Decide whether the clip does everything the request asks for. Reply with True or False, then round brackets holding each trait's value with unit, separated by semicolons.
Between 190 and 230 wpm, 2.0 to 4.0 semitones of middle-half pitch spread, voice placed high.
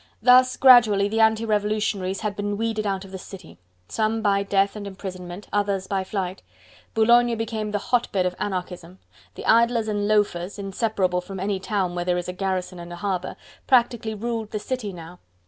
False (180 wpm; 2.8 semitones; 205 Hz)